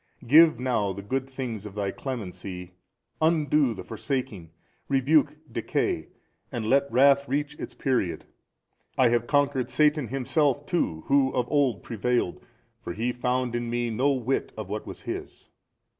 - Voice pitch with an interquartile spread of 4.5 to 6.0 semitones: No, average, 3.9 semitones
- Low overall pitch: Yes, low, 125 Hz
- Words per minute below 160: Yes, average, 150 wpm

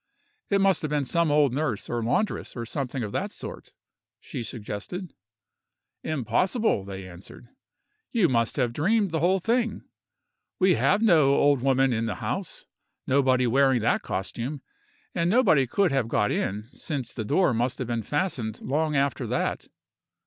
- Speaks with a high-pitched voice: No, low, 135 Hz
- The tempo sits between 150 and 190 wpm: Yes, average, 160 wpm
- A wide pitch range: Yes, wide, 6.3 semitones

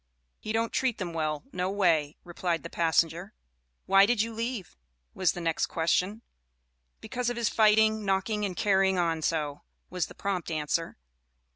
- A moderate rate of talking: Yes, average, 160 wpm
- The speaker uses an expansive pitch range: No, average, 4.5 semitones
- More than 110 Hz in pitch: Yes, medium, 185 Hz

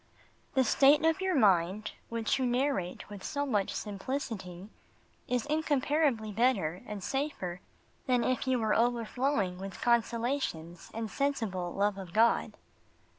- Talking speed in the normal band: No, slow, 130 wpm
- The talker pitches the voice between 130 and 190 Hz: No, high, 230 Hz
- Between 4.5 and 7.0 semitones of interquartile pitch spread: Yes, wide, 5.5 semitones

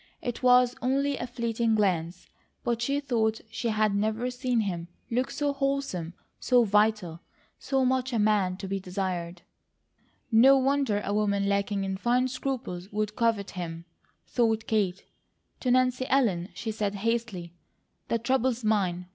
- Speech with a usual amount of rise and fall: Yes, average, 4.2 semitones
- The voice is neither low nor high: No, high, 220 Hz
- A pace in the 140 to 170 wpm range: Yes, average, 150 wpm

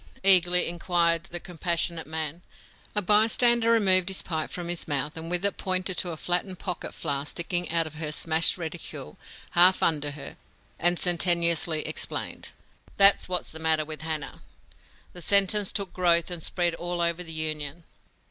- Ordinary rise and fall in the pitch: No, narrow, 2.3 semitones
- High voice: No, medium, 170 Hz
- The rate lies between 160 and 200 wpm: Yes, average, 165 wpm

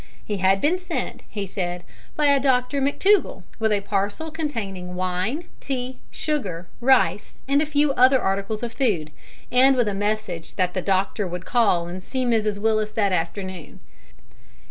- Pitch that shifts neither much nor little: No, wide, 6.0 semitones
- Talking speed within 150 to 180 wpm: Yes, average, 165 wpm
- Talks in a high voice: Yes, high, 215 Hz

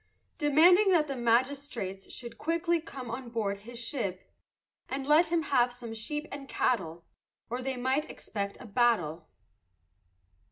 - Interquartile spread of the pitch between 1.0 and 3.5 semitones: No, average, 4.7 semitones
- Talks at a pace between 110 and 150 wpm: Yes, average, 145 wpm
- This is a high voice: Yes, very high, 250 Hz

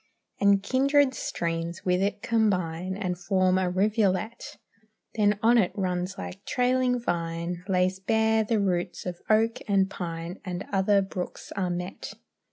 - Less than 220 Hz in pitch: Yes, high, 190 Hz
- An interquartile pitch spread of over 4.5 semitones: No, average, 3.3 semitones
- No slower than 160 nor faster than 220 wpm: No, average, 145 wpm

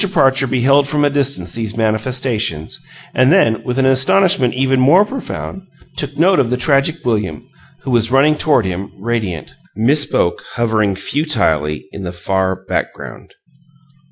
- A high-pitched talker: No, low, 125 Hz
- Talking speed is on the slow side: No, average, 150 wpm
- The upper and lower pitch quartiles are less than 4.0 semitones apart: No, wide, 5.5 semitones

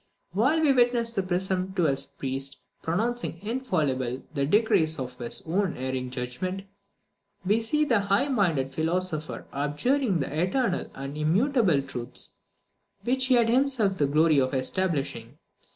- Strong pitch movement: Yes, wide, 8.6 semitones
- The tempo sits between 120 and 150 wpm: Yes, slow, 135 wpm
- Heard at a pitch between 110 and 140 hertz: No, medium, 180 Hz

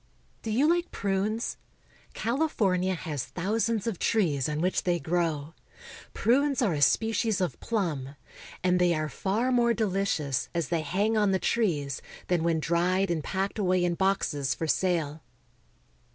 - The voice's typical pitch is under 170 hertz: No, medium, 185 Hz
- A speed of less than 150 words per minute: No, average, 155 wpm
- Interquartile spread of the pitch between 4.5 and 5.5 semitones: Yes, average, 5.0 semitones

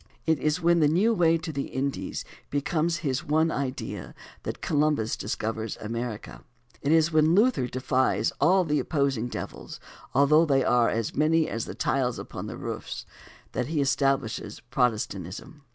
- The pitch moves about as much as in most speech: Yes, average, 4.5 semitones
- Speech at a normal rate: Yes, average, 155 wpm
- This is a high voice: No, medium, 140 Hz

